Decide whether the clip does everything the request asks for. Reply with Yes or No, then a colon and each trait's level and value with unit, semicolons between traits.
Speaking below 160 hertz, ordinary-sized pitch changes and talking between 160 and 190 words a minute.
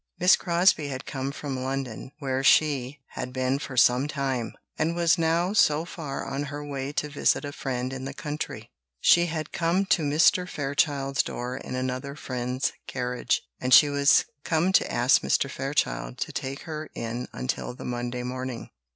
Yes: medium, 140 Hz; average, 3.1 semitones; average, 175 wpm